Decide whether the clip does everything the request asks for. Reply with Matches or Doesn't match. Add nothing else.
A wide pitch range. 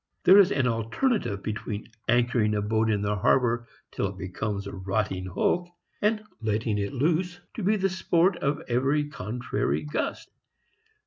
Matches